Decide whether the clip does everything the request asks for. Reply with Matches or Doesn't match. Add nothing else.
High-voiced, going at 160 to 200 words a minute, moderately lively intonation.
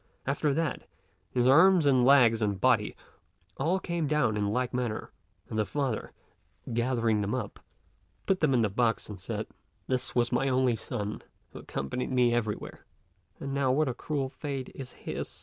Doesn't match